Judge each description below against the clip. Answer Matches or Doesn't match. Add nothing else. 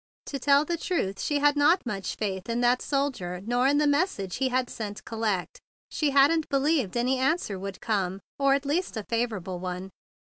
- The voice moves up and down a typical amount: Doesn't match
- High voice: Matches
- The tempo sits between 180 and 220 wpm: Matches